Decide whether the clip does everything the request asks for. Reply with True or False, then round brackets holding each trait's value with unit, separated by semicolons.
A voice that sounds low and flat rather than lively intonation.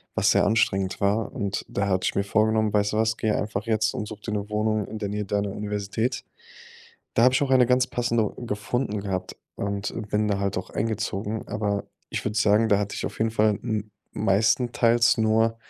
True (105 Hz; 1.7 semitones)